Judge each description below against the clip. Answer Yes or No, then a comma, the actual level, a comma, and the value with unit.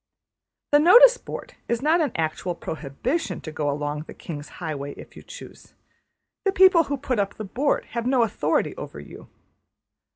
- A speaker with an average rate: Yes, average, 170 wpm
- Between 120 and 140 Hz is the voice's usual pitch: No, high, 230 Hz